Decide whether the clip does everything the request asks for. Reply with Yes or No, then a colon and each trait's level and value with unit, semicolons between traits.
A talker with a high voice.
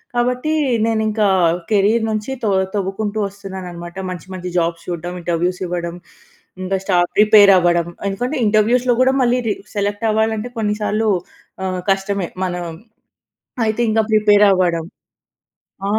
Yes: high, 205 Hz